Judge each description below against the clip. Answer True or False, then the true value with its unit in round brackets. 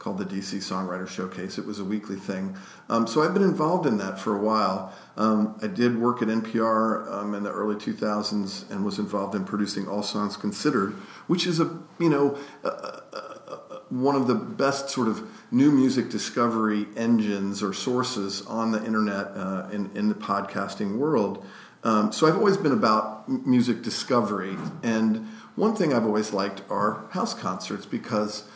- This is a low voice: True (110 Hz)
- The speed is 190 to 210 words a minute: False (180 wpm)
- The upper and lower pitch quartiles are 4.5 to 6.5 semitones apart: False (3.7 semitones)